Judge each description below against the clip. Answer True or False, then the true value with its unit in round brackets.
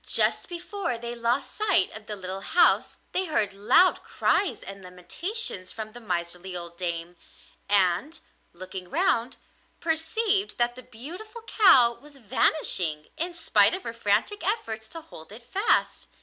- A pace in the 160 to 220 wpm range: False (150 wpm)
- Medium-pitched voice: False (235 Hz)